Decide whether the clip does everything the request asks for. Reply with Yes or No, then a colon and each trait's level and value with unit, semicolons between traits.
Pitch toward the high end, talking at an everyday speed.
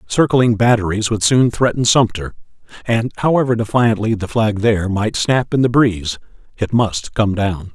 No: low, 110 Hz; average, 165 wpm